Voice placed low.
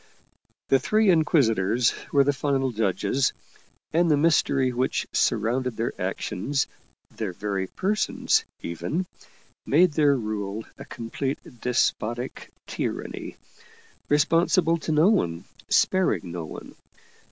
Yes: low, 130 Hz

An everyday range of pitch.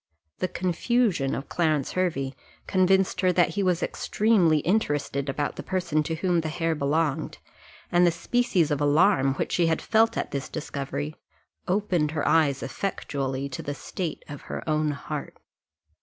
Yes: average, 4.2 semitones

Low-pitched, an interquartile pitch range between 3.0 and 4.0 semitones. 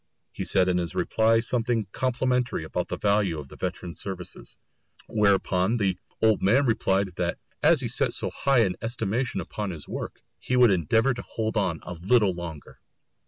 No: low, 100 Hz; average, 4.4 semitones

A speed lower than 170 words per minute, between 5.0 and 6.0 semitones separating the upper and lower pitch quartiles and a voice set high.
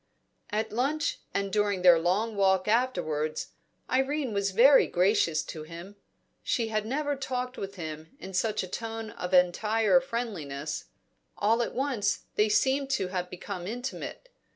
Yes: average, 150 wpm; wide, 5.4 semitones; high, 210 Hz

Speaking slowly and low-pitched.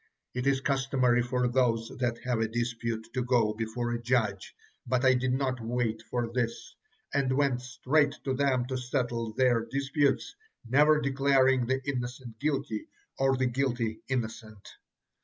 No: average, 155 wpm; low, 125 Hz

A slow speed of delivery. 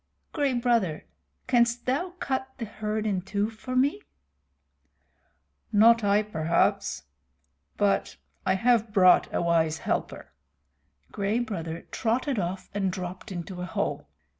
Yes: slow, 125 wpm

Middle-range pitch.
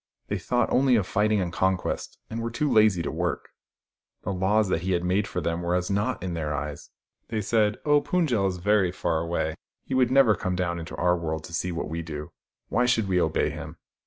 No: very low, 95 Hz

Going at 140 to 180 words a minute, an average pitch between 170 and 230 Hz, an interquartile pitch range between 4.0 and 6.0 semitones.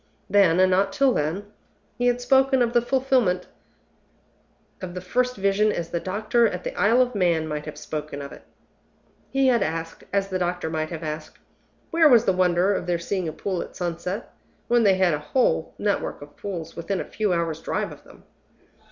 No: average, 200 wpm; medium, 185 Hz; wide, 5.6 semitones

